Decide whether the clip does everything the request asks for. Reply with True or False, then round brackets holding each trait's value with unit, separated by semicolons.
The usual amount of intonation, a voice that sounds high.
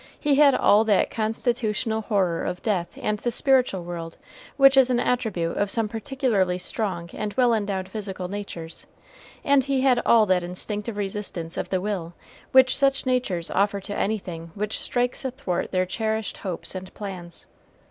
True (4.8 semitones; 210 Hz)